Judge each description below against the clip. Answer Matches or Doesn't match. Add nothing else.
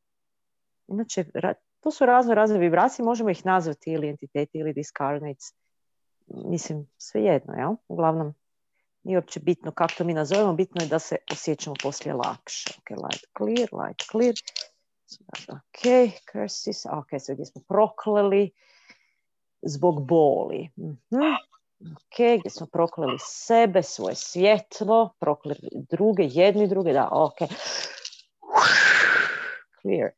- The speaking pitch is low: Doesn't match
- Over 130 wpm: Doesn't match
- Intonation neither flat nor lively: Doesn't match